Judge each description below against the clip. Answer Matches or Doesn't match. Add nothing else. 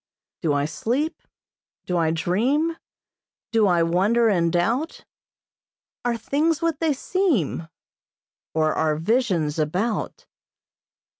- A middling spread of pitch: Doesn't match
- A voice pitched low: Doesn't match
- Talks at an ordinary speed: Doesn't match